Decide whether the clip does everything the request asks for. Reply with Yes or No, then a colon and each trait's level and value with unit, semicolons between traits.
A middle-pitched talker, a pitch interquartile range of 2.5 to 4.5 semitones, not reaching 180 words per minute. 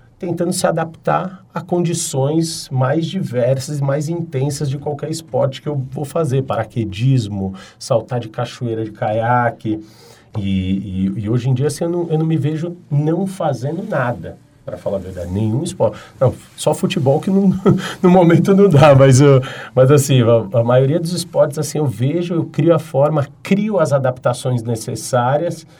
No: medium, 145 Hz; wide, 5.4 semitones; average, 170 wpm